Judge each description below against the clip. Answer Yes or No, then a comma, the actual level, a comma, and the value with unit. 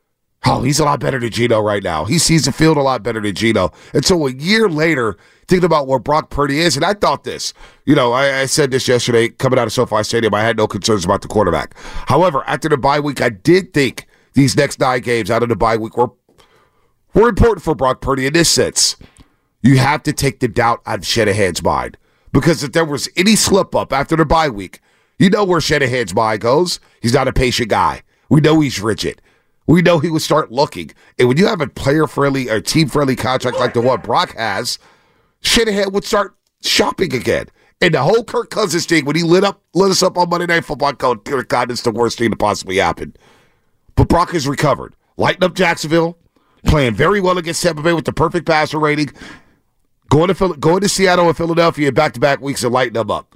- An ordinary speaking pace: No, fast, 225 wpm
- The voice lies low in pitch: No, medium, 145 Hz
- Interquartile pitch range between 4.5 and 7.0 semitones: Yes, average, 5.3 semitones